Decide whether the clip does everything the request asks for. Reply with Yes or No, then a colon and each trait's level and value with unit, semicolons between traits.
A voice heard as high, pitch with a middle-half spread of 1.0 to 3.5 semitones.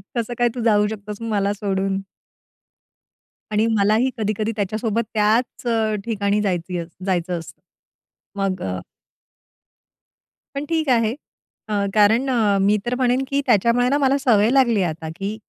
Yes: high, 215 Hz; average, 3.1 semitones